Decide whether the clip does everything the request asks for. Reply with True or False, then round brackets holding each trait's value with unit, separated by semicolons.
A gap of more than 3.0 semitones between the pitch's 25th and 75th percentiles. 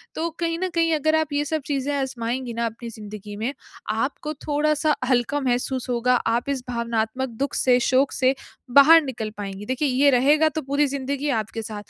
True (3.7 semitones)